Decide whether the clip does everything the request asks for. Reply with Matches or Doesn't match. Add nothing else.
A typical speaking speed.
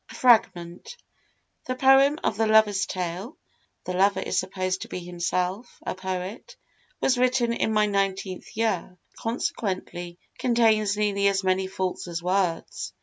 Matches